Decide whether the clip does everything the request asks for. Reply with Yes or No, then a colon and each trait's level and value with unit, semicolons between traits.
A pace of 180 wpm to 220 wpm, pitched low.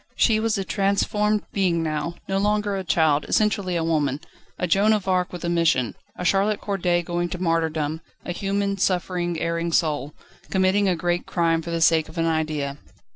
No: average, 185 wpm; medium, 175 Hz